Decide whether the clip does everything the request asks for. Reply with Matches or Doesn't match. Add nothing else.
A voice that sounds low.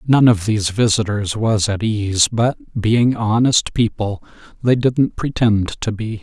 Matches